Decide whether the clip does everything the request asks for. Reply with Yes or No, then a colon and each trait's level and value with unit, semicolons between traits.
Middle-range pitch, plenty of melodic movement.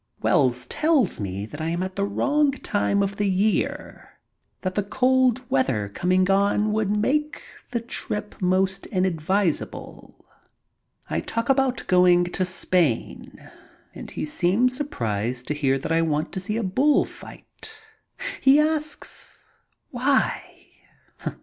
No: high, 195 Hz; wide, 6.9 semitones